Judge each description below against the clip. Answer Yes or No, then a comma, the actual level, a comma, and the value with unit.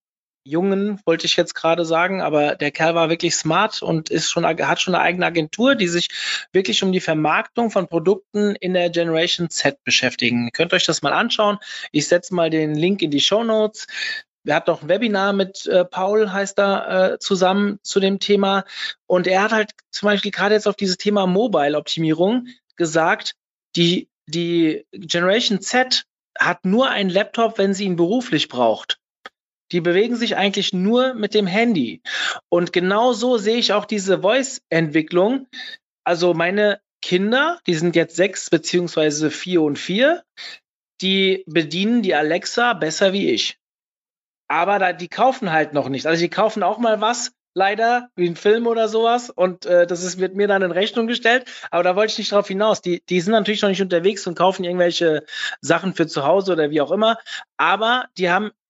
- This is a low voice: No, high, 190 Hz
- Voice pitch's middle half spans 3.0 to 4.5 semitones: Yes, average, 3.7 semitones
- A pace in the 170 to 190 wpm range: Yes, average, 185 wpm